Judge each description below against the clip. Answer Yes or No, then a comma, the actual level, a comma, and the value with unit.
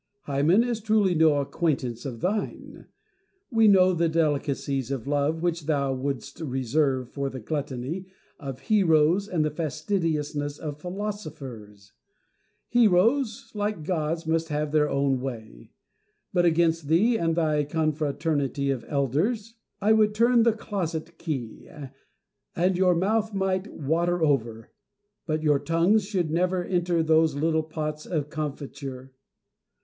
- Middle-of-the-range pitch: Yes, medium, 160 Hz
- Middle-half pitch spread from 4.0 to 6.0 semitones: Yes, average, 4.5 semitones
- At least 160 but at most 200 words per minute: No, slow, 135 wpm